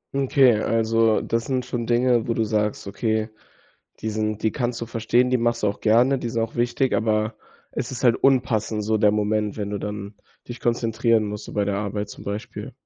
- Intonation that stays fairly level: Yes, narrow, 2.0 semitones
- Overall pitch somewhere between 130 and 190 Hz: No, low, 110 Hz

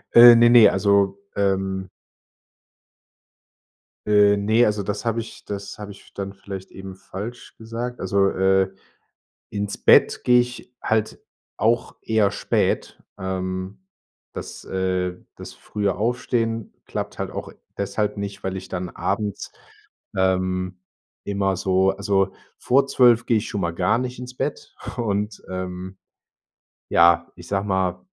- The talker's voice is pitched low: Yes, low, 100 Hz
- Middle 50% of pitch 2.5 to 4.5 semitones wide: Yes, average, 2.8 semitones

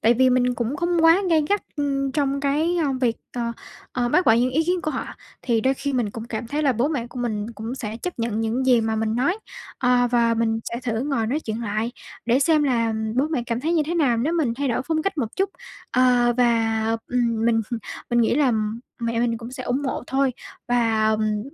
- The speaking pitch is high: Yes, high, 245 Hz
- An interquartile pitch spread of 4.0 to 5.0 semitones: No, average, 3.5 semitones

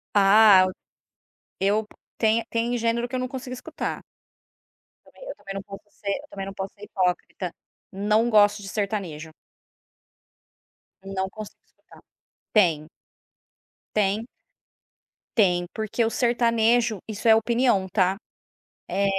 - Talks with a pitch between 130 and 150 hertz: No, high, 210 Hz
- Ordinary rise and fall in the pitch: Yes, average, 3.0 semitones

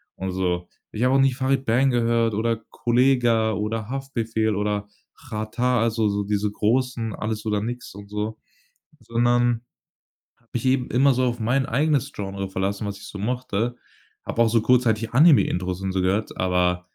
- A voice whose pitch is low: Yes, low, 115 Hz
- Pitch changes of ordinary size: Yes, average, 3.3 semitones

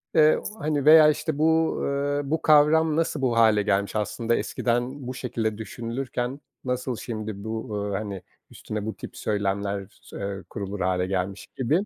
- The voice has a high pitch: No, low, 115 Hz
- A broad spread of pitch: Yes, wide, 5.7 semitones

